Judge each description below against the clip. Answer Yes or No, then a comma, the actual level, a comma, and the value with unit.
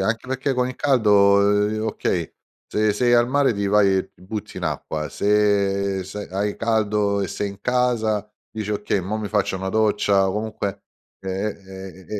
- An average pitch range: No, narrow, 2.0 semitones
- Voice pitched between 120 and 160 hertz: No, low, 105 Hz